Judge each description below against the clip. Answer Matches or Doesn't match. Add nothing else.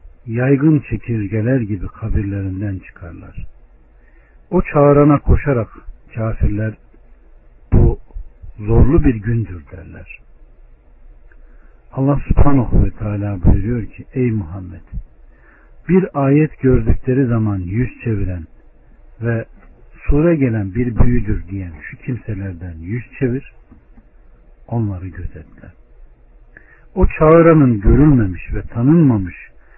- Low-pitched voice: Matches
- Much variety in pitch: Matches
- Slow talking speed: Matches